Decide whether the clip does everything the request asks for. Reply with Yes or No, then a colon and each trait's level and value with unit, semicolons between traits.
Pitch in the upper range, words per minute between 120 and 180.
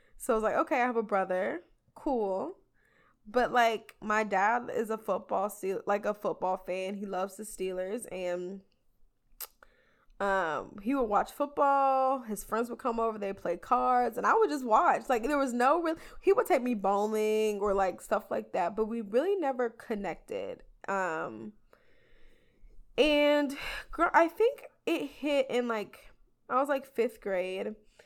Yes: high, 225 Hz; average, 170 wpm